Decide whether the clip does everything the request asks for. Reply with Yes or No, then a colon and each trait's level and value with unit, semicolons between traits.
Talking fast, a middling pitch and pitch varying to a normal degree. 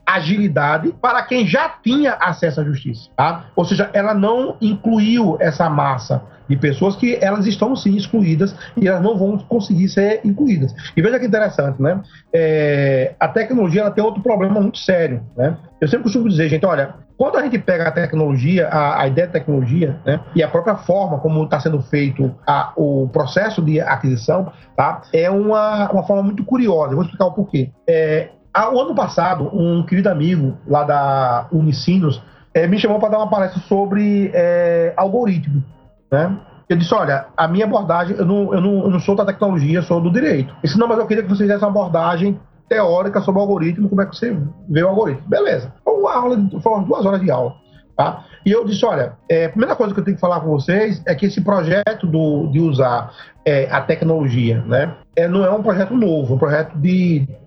Yes: fast, 205 wpm; medium, 180 Hz; average, 5.0 semitones